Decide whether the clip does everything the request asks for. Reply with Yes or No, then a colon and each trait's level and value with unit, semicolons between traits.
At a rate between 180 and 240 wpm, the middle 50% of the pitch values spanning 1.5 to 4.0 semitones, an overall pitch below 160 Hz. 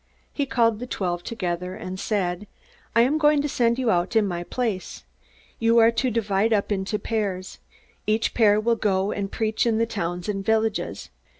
No: average, 185 wpm; average, 3.3 semitones; high, 215 Hz